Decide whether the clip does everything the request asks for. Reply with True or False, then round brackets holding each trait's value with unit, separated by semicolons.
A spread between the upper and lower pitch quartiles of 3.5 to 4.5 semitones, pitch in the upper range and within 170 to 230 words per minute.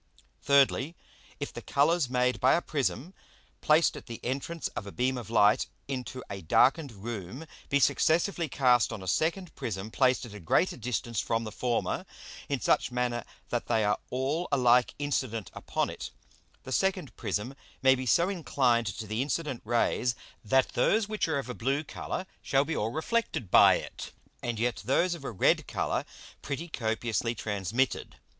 False (4.0 semitones; 125 Hz; 175 wpm)